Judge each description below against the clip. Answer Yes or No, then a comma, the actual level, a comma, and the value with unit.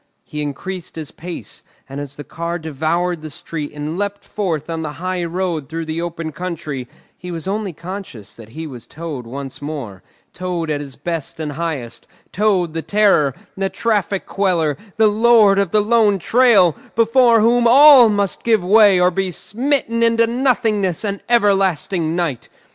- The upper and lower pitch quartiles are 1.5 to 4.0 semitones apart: No, average, 5.0 semitones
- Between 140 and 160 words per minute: No, average, 170 wpm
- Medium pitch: Yes, medium, 180 Hz